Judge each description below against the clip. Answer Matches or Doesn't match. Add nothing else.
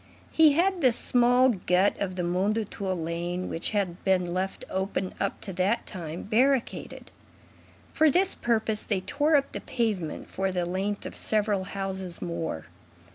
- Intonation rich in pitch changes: Doesn't match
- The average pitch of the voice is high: Matches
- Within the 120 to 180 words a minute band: Matches